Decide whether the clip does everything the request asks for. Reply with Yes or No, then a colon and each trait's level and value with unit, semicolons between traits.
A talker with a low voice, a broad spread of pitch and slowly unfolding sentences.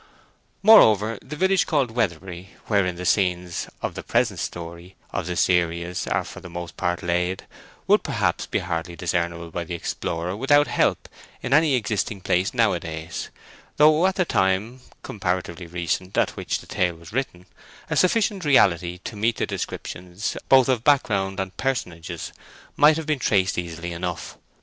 No: very low, 95 Hz; wide, 5.9 semitones; average, 160 wpm